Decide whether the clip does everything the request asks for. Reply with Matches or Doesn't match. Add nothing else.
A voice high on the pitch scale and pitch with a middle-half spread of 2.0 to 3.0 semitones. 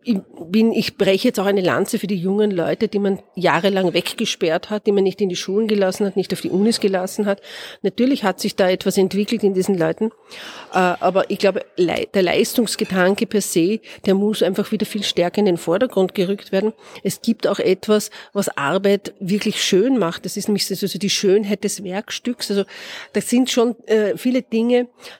Matches